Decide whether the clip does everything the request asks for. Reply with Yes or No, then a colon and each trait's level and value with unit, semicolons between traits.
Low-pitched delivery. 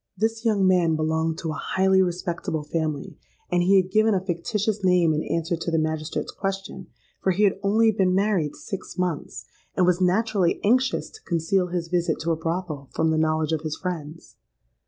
No: medium, 180 Hz